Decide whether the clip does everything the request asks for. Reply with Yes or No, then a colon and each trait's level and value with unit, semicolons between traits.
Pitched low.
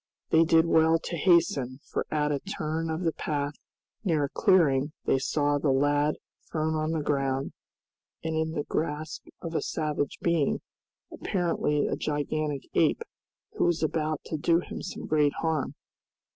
No: medium, 155 Hz